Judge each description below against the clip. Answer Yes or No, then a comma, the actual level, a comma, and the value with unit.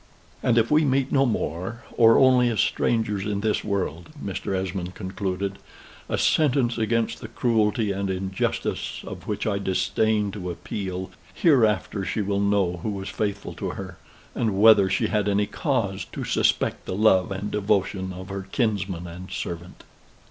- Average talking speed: Yes, average, 160 wpm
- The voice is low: Yes, low, 100 Hz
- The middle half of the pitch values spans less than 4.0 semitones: Yes, average, 2.8 semitones